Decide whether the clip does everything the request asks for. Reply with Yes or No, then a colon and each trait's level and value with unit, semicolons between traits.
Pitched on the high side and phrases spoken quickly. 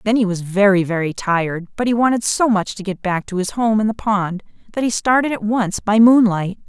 Yes: high, 205 Hz; fast, 245 wpm